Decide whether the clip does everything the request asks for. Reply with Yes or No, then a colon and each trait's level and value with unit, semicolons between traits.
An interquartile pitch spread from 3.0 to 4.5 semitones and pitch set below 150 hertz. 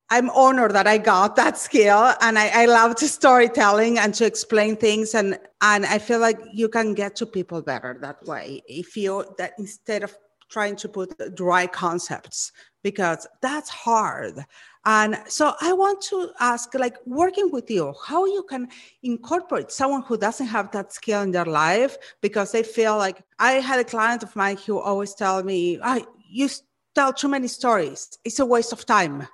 No: average, 3.9 semitones; high, 220 Hz